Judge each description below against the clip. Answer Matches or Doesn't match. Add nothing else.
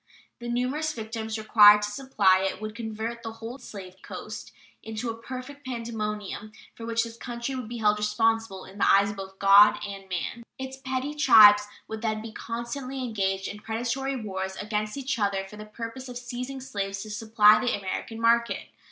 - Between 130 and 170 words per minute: Doesn't match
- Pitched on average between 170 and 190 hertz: Doesn't match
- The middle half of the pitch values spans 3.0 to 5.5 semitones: Doesn't match